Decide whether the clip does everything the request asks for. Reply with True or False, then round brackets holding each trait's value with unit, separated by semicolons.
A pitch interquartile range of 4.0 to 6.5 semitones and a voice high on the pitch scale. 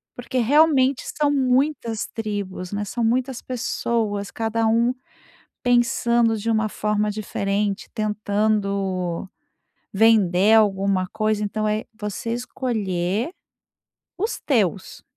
False (2.9 semitones; 215 Hz)